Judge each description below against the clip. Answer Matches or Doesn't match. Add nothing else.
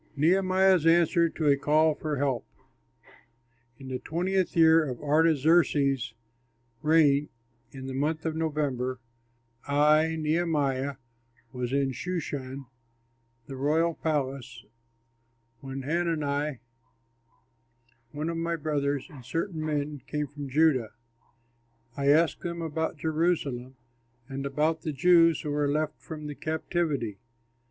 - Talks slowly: Matches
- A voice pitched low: Doesn't match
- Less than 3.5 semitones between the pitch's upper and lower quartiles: Matches